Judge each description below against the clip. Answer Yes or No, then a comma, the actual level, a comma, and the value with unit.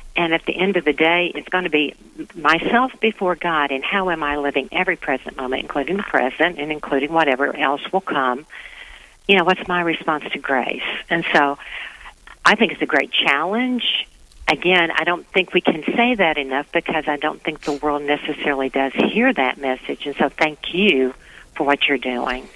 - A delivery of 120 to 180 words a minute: No, average, 195 wpm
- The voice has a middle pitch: Yes, medium, 160 Hz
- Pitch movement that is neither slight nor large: Yes, average, 4.4 semitones